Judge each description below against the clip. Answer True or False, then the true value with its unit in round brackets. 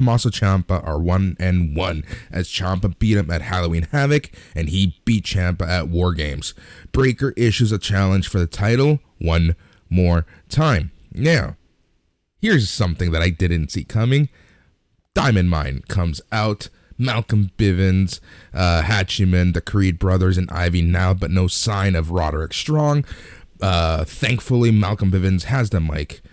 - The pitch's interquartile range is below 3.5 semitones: False (4.0 semitones)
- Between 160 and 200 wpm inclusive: False (145 wpm)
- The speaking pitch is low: True (95 Hz)